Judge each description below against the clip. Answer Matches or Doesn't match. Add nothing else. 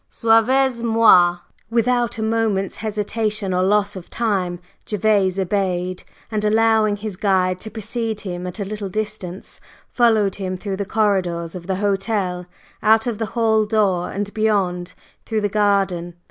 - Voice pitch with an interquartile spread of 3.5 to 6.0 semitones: Doesn't match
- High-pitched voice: Matches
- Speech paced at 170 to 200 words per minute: Doesn't match